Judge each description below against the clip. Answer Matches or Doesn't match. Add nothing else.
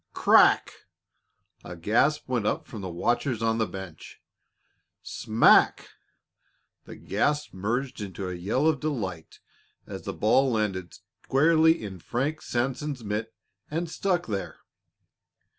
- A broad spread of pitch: Matches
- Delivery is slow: Matches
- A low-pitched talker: Matches